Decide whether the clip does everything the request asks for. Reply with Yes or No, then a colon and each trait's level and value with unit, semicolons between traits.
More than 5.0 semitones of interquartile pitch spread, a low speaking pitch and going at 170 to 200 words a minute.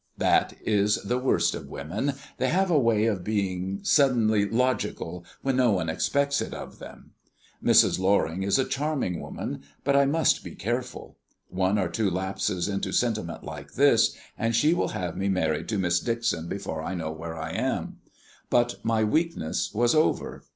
Yes: wide, 5.5 semitones; low, 105 Hz; average, 175 wpm